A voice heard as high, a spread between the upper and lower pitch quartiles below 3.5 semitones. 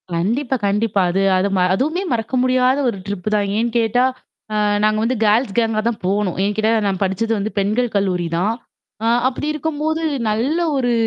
No: high, 225 Hz; average, 4.0 semitones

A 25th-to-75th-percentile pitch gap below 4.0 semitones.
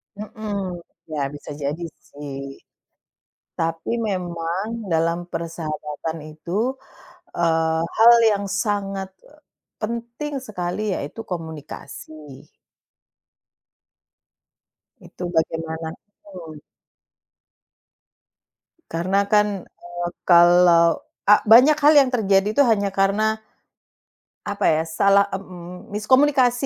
No: average, 4.3 semitones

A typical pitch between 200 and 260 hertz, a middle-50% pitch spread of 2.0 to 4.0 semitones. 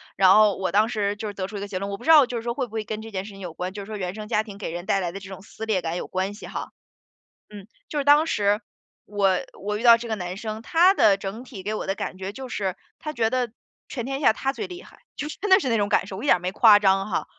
Yes: high, 210 Hz; average, 3.4 semitones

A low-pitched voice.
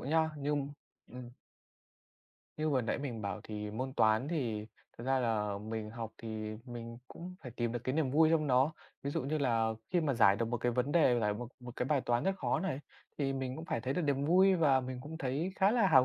Yes: low, 130 Hz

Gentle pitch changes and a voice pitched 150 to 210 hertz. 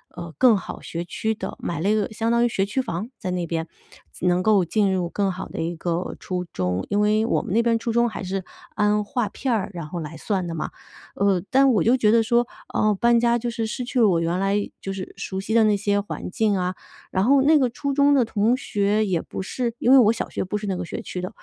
No: average, 4.2 semitones; high, 205 Hz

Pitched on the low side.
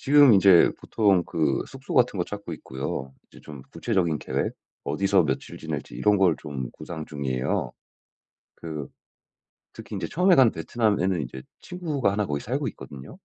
Yes: very low, 90 Hz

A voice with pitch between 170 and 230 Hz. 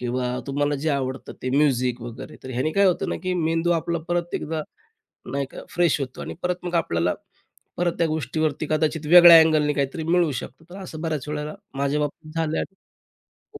No: medium, 155 Hz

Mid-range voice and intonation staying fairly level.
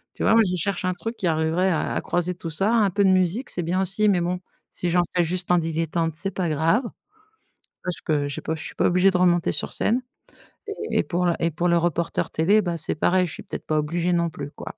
Yes: medium, 175 Hz; narrow, 2.2 semitones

